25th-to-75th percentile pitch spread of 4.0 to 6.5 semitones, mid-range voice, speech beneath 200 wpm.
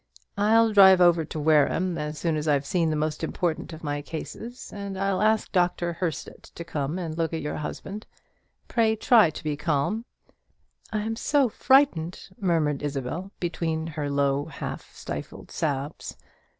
Yes: average, 4.6 semitones; medium, 165 Hz; average, 165 wpm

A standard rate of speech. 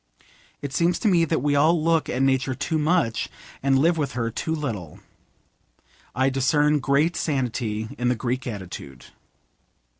Yes: average, 155 wpm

